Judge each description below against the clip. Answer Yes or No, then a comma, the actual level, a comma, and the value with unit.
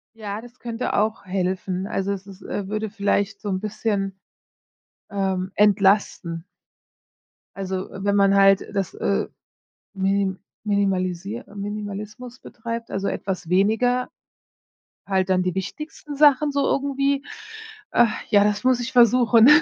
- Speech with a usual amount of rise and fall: Yes, average, 3.1 semitones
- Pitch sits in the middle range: No, high, 200 Hz